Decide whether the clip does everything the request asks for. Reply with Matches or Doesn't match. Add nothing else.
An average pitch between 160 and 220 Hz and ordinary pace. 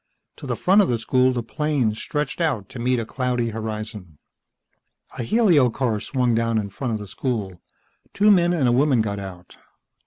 Doesn't match